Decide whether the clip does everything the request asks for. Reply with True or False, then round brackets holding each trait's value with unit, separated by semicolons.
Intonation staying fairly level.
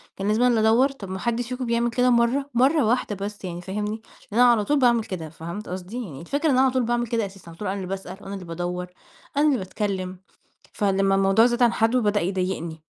False (4.2 semitones)